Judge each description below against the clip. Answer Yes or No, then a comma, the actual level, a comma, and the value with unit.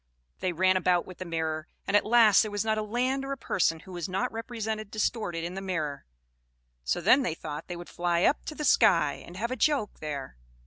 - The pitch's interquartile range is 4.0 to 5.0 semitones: Yes, average, 4.7 semitones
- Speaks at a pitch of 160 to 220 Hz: Yes, high, 190 Hz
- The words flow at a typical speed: No, fast, 230 wpm